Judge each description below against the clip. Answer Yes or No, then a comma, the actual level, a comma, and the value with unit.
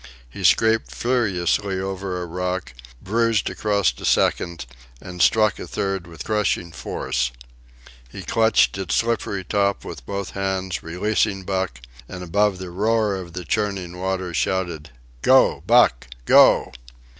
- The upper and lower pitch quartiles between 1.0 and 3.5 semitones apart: Yes, average, 2.8 semitones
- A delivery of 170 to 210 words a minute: No, slow, 135 wpm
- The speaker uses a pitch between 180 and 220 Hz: No, very low, 95 Hz